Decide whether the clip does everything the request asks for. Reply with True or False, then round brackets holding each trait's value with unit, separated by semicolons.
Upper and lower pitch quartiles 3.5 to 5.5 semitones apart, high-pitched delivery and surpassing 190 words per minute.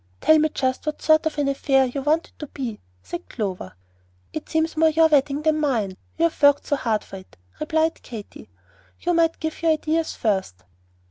True (4.4 semitones; 295 Hz; 200 wpm)